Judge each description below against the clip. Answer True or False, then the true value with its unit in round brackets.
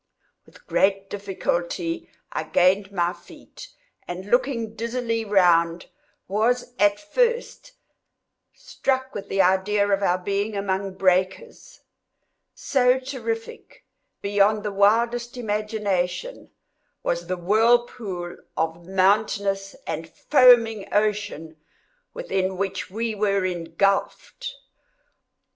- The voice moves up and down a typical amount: True (3.5 semitones)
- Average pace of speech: False (100 wpm)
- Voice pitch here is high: True (205 Hz)